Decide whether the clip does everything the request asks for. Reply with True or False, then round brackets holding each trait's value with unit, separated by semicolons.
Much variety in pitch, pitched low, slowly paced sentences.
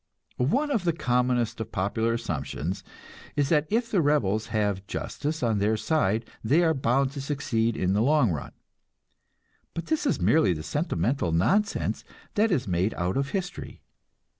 False (7.3 semitones; 125 Hz; 165 wpm)